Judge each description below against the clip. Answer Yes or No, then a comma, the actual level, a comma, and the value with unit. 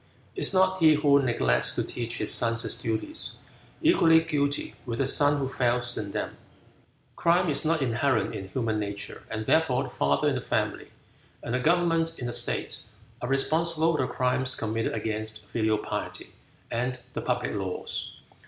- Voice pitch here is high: No, low, 125 Hz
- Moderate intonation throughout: No, wide, 5.9 semitones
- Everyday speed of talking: Yes, average, 170 wpm